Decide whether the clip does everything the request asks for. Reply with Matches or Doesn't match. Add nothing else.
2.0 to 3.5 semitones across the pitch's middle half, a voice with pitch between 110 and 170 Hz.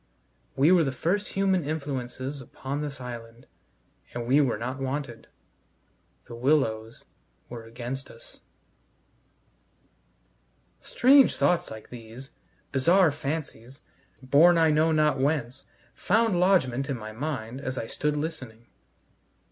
Doesn't match